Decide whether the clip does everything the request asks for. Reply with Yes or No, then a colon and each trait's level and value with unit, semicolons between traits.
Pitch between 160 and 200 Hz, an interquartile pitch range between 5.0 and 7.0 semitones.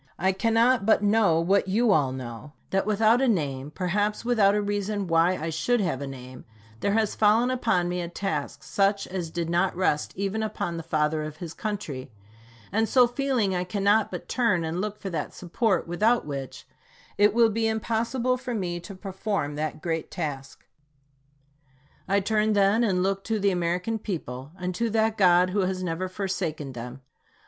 No: high, 190 Hz; average, 4.6 semitones